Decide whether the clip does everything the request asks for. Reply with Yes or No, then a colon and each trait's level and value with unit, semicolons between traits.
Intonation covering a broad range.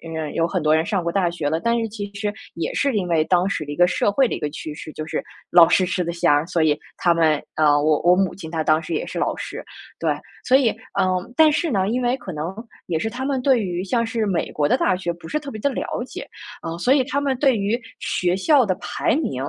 Yes: wide, 6.1 semitones